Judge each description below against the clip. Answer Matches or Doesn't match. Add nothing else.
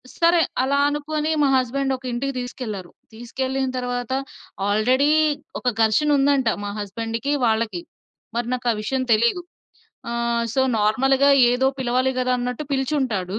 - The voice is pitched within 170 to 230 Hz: Doesn't match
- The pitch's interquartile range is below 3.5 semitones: Matches